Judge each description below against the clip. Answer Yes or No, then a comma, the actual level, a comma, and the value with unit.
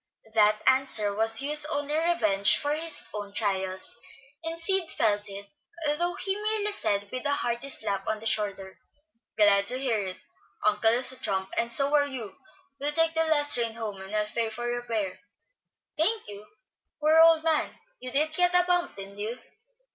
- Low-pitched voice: No, high, 240 Hz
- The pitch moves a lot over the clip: Yes, wide, 7.0 semitones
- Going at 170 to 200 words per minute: Yes, average, 180 wpm